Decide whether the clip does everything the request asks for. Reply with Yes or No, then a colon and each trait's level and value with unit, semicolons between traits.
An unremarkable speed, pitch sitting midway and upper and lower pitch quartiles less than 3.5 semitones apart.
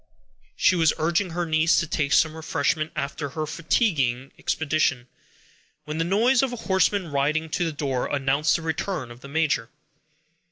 Yes: average, 165 wpm; medium, 155 Hz; average, 3.0 semitones